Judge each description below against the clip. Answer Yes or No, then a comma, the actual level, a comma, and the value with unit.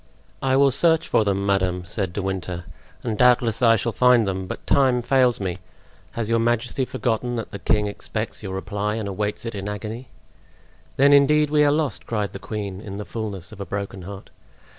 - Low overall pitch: Yes, low, 110 Hz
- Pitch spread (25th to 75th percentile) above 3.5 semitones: Yes, average, 3.9 semitones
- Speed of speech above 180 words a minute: Yes, average, 200 wpm